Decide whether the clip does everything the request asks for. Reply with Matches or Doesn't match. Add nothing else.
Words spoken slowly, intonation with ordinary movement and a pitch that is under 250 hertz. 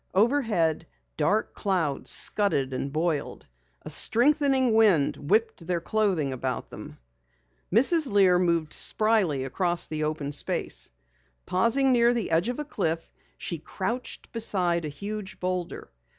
Doesn't match